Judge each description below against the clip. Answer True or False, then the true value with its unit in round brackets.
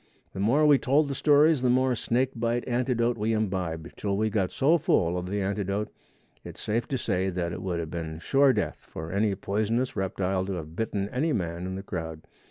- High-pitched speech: False (105 Hz)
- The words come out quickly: True (210 wpm)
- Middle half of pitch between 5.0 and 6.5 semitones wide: True (5.5 semitones)